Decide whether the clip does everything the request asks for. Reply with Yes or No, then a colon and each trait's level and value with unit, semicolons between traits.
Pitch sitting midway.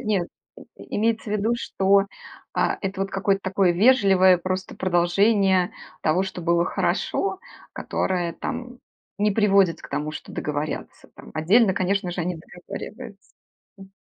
No: high, 195 Hz